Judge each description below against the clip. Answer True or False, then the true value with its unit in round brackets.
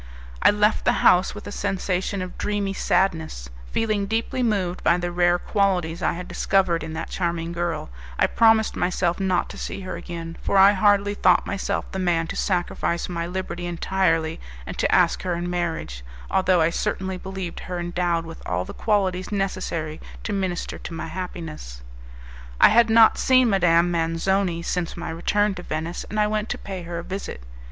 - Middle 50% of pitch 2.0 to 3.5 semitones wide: True (2.7 semitones)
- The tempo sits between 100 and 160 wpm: False (185 wpm)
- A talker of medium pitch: True (180 Hz)